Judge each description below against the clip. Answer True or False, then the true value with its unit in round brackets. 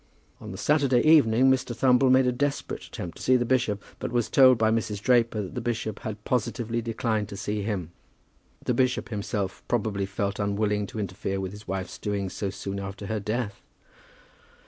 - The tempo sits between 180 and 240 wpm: True (190 wpm)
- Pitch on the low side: True (110 Hz)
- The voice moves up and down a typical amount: True (3.4 semitones)